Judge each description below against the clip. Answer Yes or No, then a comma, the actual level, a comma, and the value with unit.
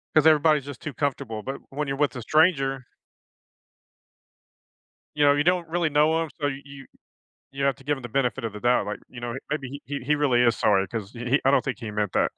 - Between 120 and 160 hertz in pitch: Yes, low, 135 Hz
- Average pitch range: Yes, average, 3.3 semitones